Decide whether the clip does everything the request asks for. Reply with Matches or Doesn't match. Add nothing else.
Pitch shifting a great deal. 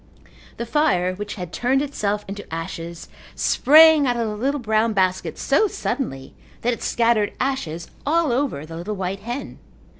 Matches